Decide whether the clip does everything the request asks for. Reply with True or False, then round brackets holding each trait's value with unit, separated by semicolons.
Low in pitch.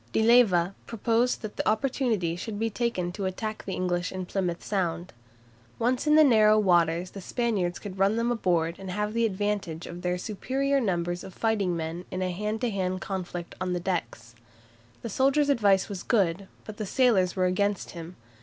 False (195 Hz)